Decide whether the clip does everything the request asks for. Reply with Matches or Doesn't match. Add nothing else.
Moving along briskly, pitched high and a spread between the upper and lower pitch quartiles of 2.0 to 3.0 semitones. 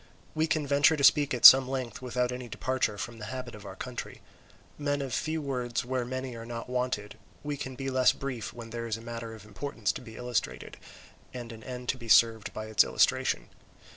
Doesn't match